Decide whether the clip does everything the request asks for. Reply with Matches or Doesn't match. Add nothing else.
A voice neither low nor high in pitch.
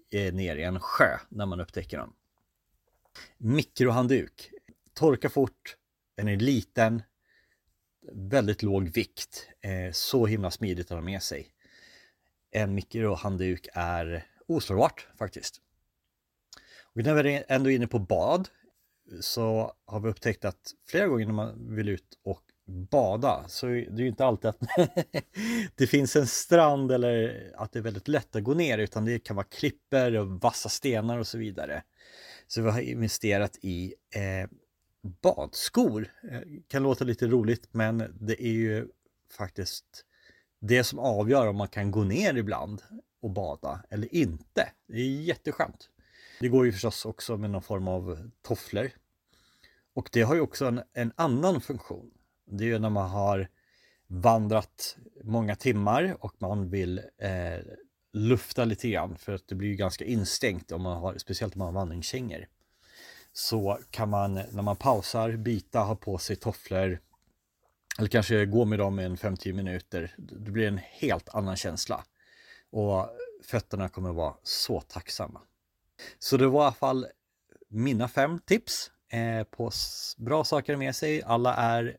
Doesn't match